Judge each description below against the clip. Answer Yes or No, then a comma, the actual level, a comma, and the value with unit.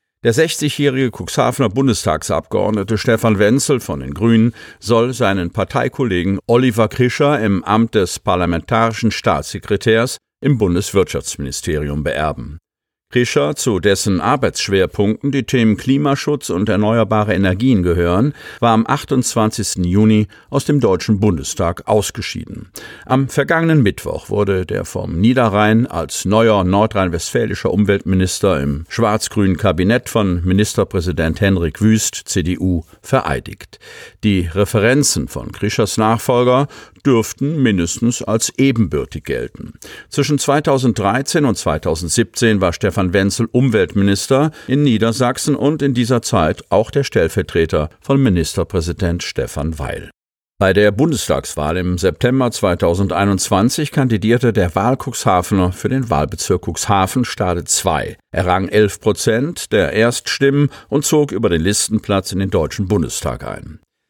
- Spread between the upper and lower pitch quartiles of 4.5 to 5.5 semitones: Yes, average, 4.9 semitones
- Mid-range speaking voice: No, low, 110 Hz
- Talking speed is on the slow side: Yes, slow, 115 wpm